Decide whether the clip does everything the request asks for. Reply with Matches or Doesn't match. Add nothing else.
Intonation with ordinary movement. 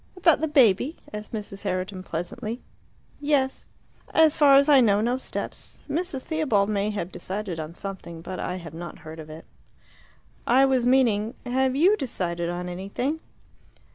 Doesn't match